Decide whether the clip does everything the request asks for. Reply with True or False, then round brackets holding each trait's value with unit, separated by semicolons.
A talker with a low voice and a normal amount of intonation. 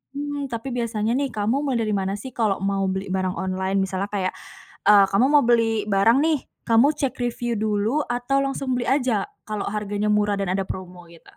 False (210 Hz; 3.8 semitones)